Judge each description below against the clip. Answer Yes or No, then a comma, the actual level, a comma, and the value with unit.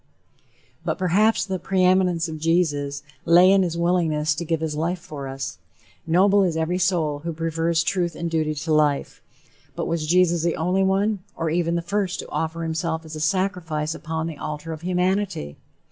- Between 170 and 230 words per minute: Yes, average, 180 wpm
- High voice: No, medium, 165 Hz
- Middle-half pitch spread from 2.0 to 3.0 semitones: Yes, narrow, 2.5 semitones